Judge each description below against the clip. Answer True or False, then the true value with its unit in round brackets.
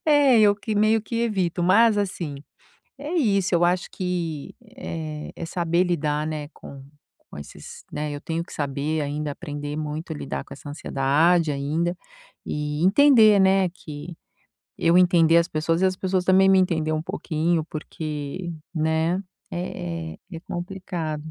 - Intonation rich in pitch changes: False (3.7 semitones)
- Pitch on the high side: False (170 Hz)